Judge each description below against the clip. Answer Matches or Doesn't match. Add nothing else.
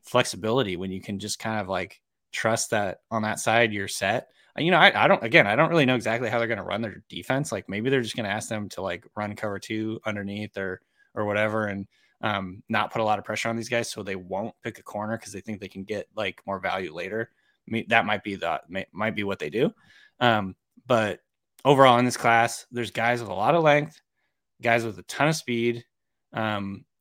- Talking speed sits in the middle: Doesn't match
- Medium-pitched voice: Doesn't match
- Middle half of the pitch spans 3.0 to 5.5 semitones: Doesn't match